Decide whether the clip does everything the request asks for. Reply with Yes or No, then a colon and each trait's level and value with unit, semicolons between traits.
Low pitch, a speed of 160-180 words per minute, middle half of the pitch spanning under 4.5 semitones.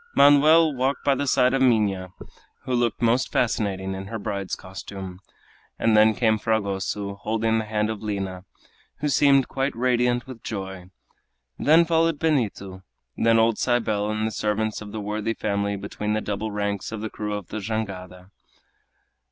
Yes: low, 110 Hz; average, 165 wpm; average, 3.4 semitones